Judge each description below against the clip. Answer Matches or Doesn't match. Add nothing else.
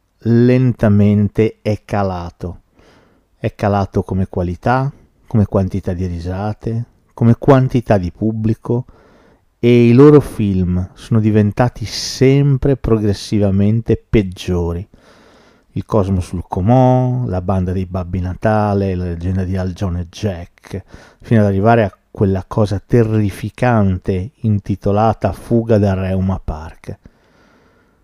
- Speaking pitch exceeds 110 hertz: Doesn't match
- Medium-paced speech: Doesn't match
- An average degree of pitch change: Matches